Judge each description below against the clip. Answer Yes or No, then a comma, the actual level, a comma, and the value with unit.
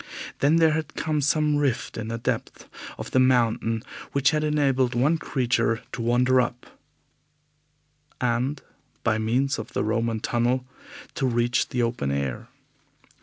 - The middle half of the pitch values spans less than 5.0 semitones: Yes, average, 3.3 semitones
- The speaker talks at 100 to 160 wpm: Yes, average, 145 wpm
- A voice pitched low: Yes, low, 125 Hz